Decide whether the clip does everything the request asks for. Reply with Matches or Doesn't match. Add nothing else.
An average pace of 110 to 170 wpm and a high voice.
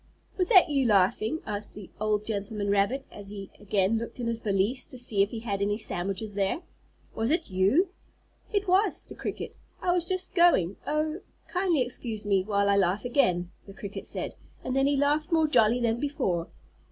Doesn't match